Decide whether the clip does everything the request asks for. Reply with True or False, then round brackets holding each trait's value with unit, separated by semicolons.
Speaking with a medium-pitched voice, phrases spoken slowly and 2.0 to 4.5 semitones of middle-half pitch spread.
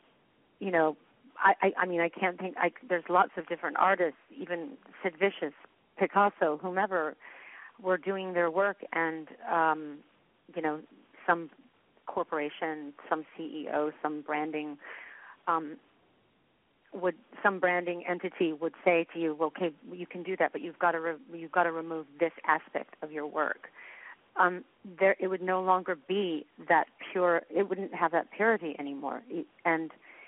False (175 Hz; 155 wpm; 2.6 semitones)